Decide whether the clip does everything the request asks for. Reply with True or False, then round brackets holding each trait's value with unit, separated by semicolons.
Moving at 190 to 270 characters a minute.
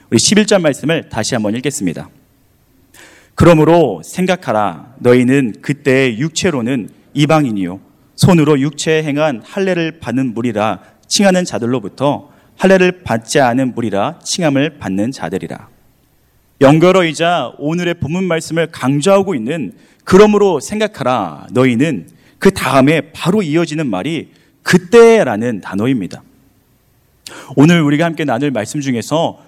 False (295 characters per minute)